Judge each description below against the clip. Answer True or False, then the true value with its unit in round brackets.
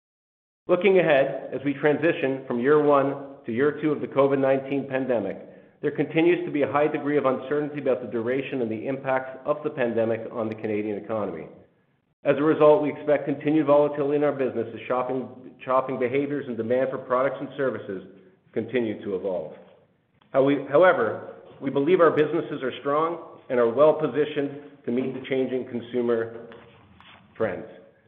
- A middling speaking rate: True (170 wpm)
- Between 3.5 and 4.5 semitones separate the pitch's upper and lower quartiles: False (2.9 semitones)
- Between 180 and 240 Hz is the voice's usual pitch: False (135 Hz)